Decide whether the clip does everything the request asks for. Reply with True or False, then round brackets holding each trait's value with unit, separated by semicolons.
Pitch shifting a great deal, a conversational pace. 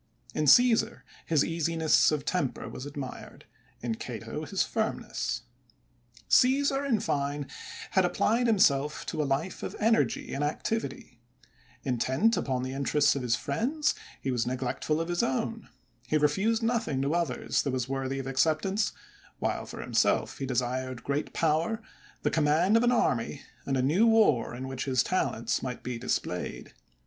True (6.7 semitones; 155 wpm)